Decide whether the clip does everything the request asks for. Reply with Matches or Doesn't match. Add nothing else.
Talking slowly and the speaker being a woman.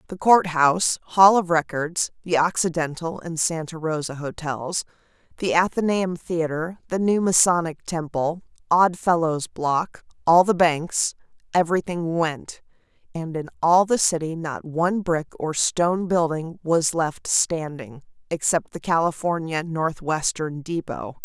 Matches